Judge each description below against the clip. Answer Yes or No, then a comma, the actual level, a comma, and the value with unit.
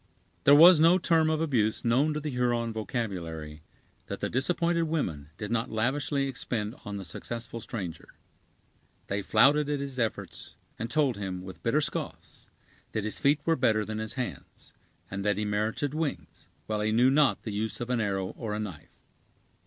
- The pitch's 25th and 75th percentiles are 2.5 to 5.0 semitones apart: No, wide, 5.5 semitones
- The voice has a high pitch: No, low, 115 Hz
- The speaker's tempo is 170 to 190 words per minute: Yes, average, 180 wpm